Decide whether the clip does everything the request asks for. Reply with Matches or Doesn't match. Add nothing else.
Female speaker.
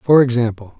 Doesn't match